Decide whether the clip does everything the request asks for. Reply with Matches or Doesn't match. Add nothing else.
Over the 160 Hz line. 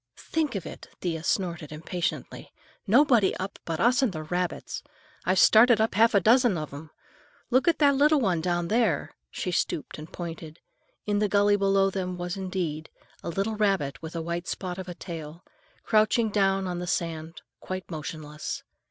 Matches